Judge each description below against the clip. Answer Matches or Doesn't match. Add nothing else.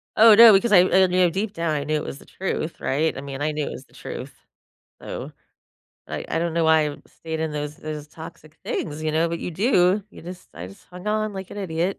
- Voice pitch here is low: Doesn't match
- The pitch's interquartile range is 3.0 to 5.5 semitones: Matches